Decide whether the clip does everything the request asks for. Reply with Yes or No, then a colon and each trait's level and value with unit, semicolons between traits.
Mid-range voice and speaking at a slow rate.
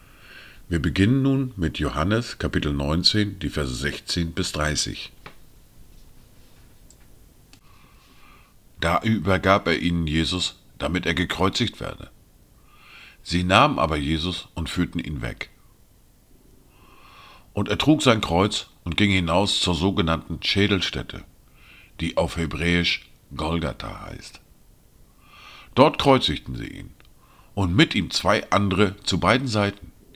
No: very low, 90 Hz; slow, 115 wpm